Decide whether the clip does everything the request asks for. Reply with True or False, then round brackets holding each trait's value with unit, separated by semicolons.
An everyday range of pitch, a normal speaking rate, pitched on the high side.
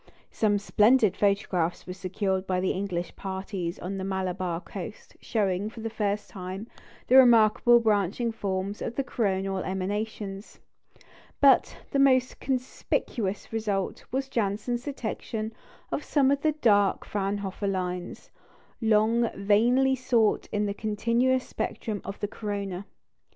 False (3.4 semitones; 130 wpm; 205 Hz)